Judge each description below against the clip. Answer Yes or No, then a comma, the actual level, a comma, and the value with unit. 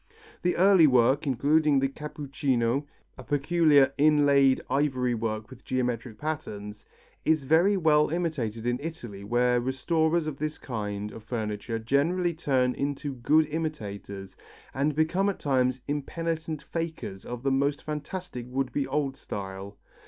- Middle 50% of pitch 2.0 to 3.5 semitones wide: No, average, 4.3 semitones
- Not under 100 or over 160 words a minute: Yes, slow, 135 wpm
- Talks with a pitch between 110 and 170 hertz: Yes, medium, 140 Hz